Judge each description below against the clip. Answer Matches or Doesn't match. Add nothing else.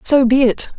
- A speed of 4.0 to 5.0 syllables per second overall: Matches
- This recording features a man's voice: Doesn't match